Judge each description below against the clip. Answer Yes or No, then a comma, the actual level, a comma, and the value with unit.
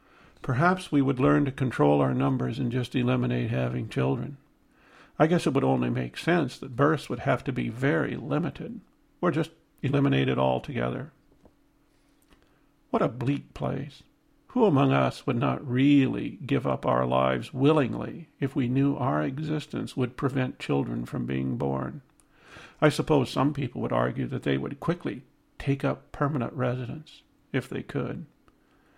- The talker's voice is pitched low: Yes, low, 130 Hz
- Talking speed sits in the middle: Yes, average, 155 wpm